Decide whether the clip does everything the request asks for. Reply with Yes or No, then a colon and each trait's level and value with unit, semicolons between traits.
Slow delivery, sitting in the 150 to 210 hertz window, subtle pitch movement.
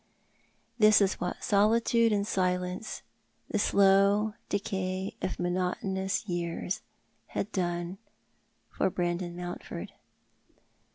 Yes: slow, 100 wpm; high, 190 Hz; narrow, 2.1 semitones